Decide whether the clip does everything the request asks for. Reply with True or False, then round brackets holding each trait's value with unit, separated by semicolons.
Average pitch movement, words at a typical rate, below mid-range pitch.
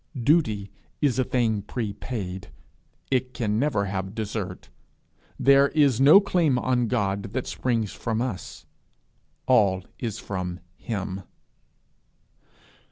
False (4.6 semitones; 110 wpm; 110 Hz)